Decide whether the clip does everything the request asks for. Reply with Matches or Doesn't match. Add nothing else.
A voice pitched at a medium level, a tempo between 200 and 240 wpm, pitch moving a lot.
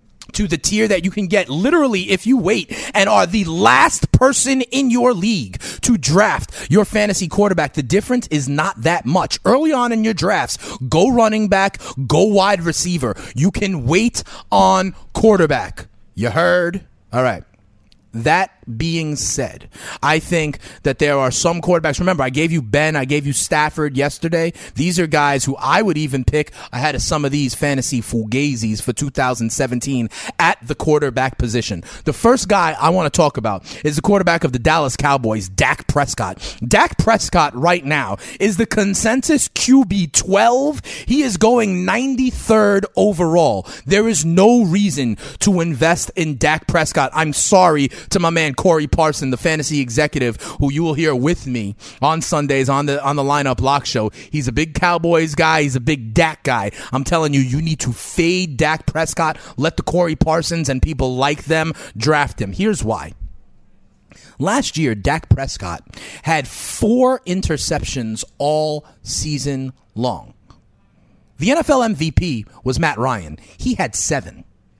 Doesn't match